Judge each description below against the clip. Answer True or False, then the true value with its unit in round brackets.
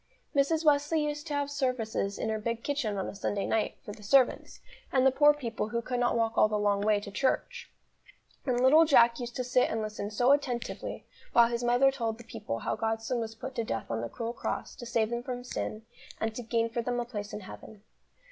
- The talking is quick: True (235 wpm)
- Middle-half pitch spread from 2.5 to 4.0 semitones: True (3.2 semitones)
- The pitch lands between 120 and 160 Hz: False (235 Hz)